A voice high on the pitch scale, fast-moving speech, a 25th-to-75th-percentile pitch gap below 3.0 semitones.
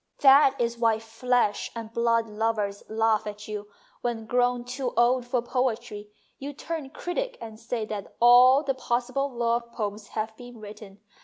No: high, 235 Hz; average, 165 wpm; narrow, 2.4 semitones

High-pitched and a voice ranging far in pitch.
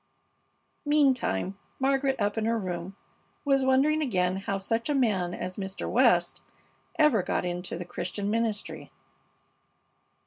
Yes: high, 215 Hz; wide, 6.2 semitones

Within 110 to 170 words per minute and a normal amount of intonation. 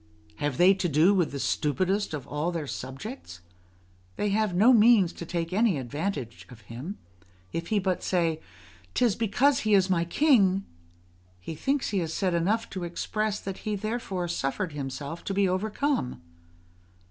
Yes: average, 165 wpm; average, 4.9 semitones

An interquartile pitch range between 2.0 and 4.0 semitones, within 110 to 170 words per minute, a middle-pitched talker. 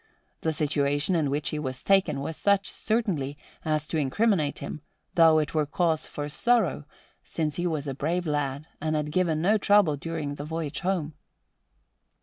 Yes: average, 3.2 semitones; average, 165 wpm; medium, 155 Hz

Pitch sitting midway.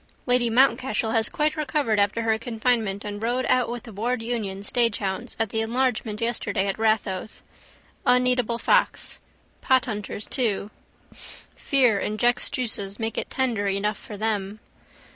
No: high, 225 Hz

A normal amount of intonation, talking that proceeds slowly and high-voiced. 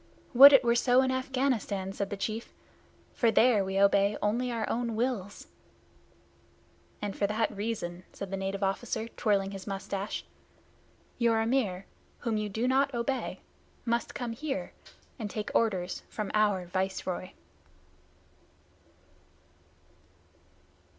Yes: average, 3.4 semitones; slow, 125 wpm; high, 215 Hz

